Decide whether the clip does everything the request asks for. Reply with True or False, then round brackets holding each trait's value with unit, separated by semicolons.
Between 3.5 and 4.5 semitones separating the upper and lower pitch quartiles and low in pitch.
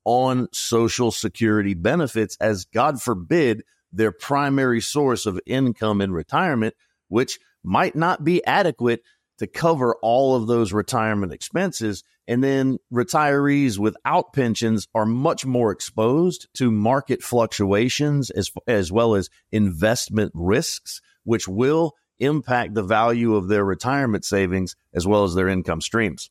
True (4.0 semitones; 115 Hz)